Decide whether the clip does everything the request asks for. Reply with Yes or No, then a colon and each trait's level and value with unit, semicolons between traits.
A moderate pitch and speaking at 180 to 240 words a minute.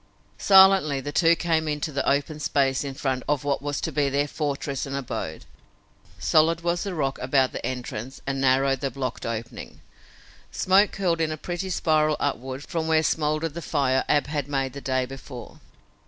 Yes: medium, 145 Hz; average, 185 wpm